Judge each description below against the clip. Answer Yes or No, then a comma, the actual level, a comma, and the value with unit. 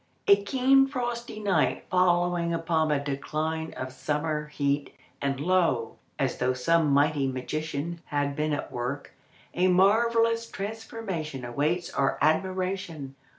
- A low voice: No, medium, 160 Hz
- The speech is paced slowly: Yes, slow, 125 wpm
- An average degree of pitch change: Yes, average, 5.0 semitones